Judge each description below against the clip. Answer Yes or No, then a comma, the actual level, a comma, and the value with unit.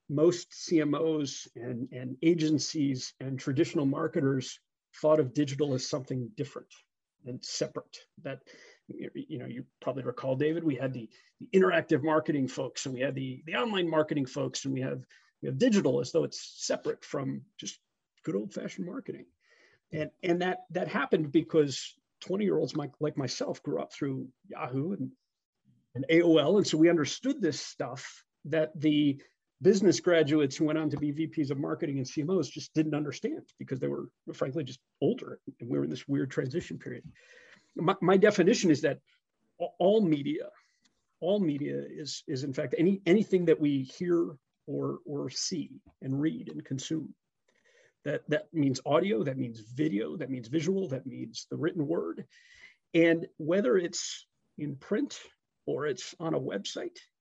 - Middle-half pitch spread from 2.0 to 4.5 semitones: Yes, average, 4.2 semitones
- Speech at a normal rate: Yes, average, 165 wpm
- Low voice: No, medium, 155 Hz